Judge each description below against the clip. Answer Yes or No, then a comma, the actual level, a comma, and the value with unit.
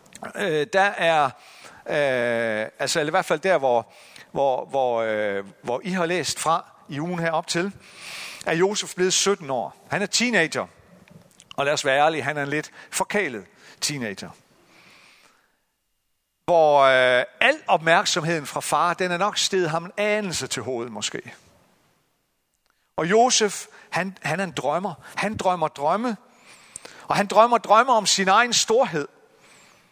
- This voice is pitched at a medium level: Yes, medium, 175 Hz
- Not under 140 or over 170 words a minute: Yes, slow, 145 wpm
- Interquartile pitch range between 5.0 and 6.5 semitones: Yes, wide, 5.4 semitones